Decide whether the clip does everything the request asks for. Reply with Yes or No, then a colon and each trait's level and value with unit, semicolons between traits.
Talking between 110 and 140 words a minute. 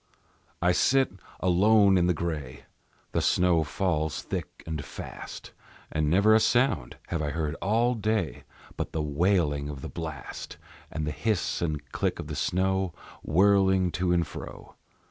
No: average, 155 wpm